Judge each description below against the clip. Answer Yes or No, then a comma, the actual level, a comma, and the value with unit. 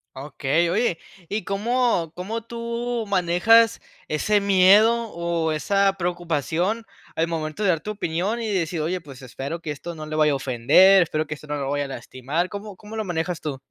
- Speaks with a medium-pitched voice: Yes, medium, 175 Hz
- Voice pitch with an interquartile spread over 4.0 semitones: Yes, average, 5.2 semitones